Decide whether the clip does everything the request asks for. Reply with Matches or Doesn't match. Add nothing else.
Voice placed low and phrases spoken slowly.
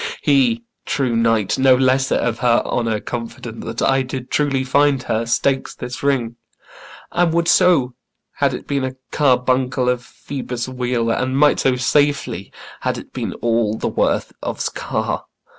Doesn't match